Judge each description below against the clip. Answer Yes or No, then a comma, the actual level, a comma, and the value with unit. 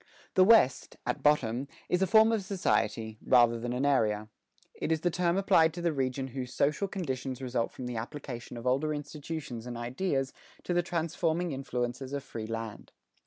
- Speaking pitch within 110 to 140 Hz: Yes, low, 135 Hz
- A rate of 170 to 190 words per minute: Yes, average, 180 wpm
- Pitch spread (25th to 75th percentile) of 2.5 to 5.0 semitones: No, wide, 5.5 semitones